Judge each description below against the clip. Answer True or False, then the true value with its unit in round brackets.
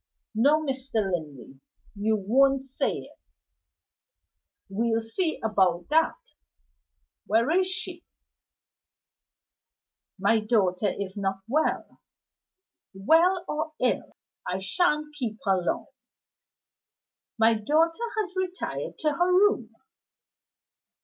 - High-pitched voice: True (245 Hz)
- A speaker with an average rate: False (95 wpm)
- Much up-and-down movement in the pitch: True (8.0 semitones)